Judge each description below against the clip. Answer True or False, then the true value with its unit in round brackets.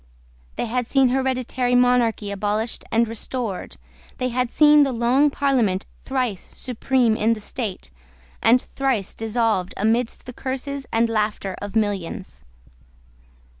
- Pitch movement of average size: True (3.1 semitones)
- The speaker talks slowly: True (130 wpm)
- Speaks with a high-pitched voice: True (235 Hz)